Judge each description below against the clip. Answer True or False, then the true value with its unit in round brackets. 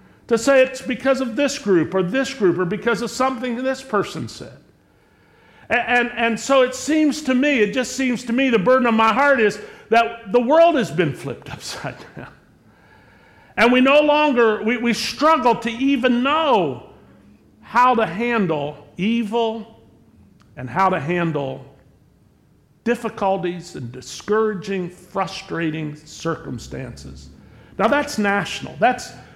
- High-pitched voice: True (225 Hz)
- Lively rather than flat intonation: True (6.2 semitones)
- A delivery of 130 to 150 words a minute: True (145 wpm)